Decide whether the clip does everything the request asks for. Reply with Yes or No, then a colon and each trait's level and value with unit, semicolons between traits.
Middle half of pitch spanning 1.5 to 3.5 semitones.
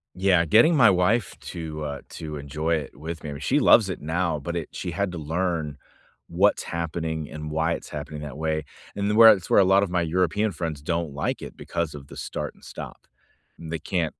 Yes: average, 3.2 semitones